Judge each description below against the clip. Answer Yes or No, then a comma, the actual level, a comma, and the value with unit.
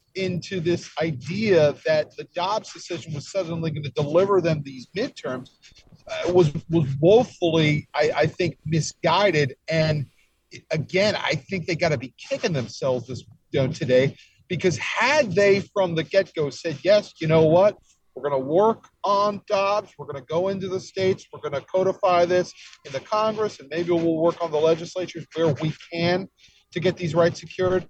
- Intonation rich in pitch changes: No, average, 3.8 semitones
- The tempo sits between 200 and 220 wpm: No, average, 180 wpm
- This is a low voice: No, medium, 170 Hz